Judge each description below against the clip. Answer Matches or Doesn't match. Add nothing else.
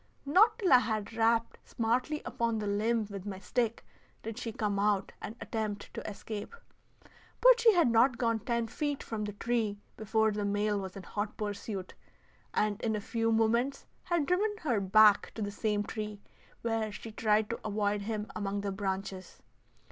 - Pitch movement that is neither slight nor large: Doesn't match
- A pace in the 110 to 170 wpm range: Doesn't match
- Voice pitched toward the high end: Matches